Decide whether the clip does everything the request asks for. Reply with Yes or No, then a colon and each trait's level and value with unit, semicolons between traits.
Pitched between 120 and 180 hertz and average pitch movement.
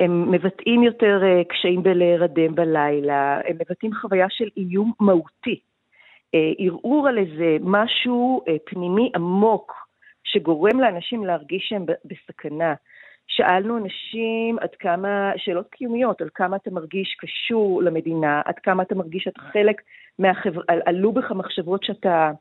No: high, 190 Hz; average, 3.7 semitones